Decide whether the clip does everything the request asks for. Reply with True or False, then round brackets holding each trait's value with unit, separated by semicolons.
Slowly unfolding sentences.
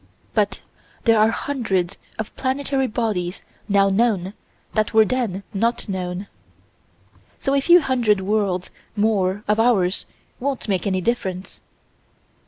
True (125 wpm)